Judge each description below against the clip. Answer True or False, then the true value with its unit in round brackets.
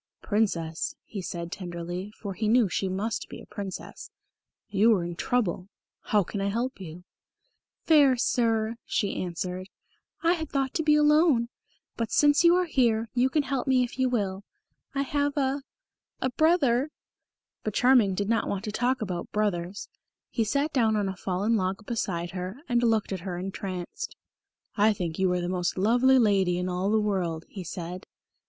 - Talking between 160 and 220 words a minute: True (180 wpm)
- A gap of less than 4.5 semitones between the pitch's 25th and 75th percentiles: False (5.3 semitones)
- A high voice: True (210 Hz)